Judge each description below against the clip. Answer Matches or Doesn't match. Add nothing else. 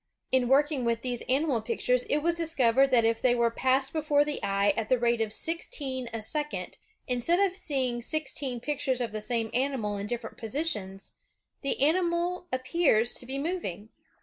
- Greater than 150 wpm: Matches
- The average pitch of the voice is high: Matches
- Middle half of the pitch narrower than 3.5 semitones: Doesn't match